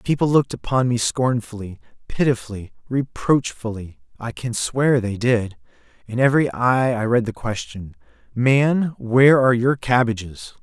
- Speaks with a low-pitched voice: Yes, low, 120 Hz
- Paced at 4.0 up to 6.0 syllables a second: Yes, 4.5 syllables/s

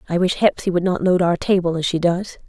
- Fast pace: Yes, fast, 265 wpm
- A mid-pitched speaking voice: Yes, medium, 180 Hz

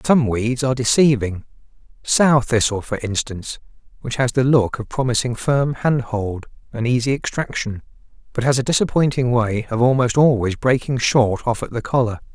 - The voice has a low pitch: Yes, low, 125 Hz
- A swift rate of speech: No, average, 160 wpm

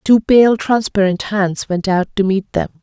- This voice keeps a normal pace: Yes, average, 190 wpm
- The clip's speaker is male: No, female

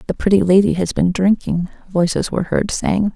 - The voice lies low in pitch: No, medium, 185 Hz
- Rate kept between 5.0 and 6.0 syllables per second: Yes, 5.4 syllables/s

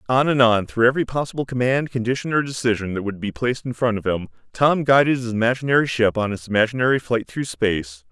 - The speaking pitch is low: Yes, low, 120 Hz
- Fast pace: Yes, fast, 215 wpm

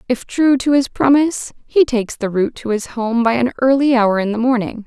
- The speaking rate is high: Yes, fast, 235 wpm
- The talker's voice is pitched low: No, high, 245 Hz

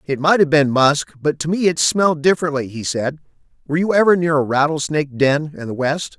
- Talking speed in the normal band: No, fast, 225 wpm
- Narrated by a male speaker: Yes, male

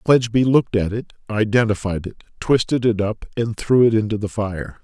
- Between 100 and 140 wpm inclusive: No, average, 185 wpm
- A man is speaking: Yes, male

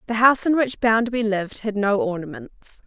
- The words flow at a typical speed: Yes, average, 190 wpm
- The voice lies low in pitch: No, high, 225 Hz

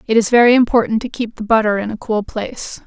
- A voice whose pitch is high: Yes, high, 225 Hz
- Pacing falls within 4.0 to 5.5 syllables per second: No, 6.3 syllables/s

